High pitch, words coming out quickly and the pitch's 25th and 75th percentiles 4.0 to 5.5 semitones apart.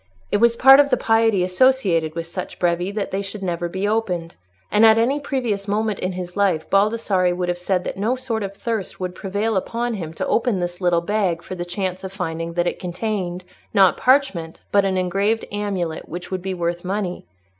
No: high, 195 Hz; fast, 210 wpm; average, 3.6 semitones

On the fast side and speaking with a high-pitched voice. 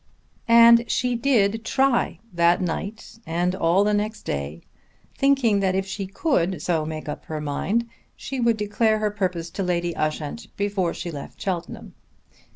No: average, 160 wpm; high, 195 Hz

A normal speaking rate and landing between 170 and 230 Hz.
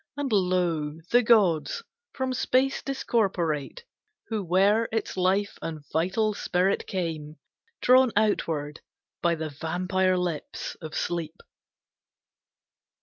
No: slow, 105 wpm; medium, 185 Hz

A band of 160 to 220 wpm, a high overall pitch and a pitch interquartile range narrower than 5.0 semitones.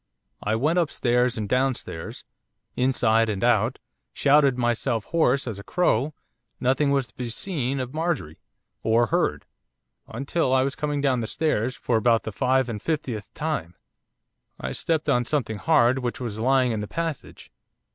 No: average, 165 wpm; low, 125 Hz; average, 3.9 semitones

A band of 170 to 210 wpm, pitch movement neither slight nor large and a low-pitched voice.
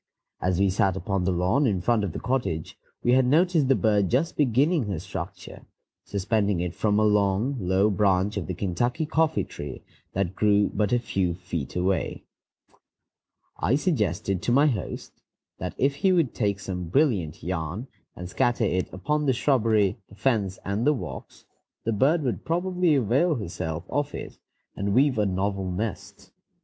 No: average, 175 wpm; wide, 6.0 semitones; low, 105 Hz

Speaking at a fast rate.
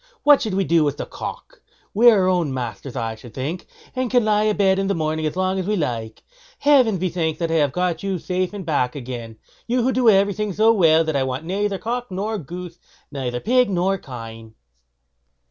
Yes: fast, 215 wpm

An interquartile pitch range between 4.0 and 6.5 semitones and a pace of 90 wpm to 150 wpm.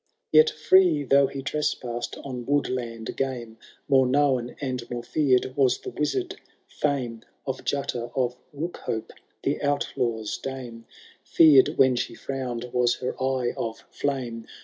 No: average, 2.8 semitones; slow, 135 wpm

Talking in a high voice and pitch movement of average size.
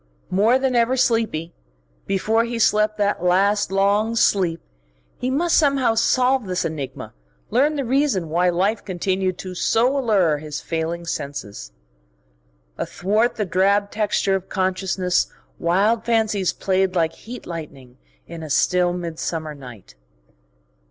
Yes: high, 195 Hz; average, 4.8 semitones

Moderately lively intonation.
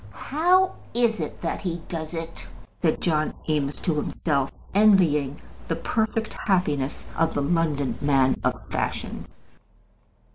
No: wide, 5.7 semitones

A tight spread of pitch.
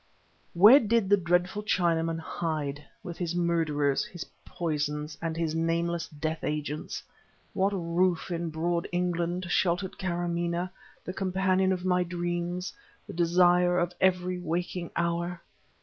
Yes: narrow, 1.5 semitones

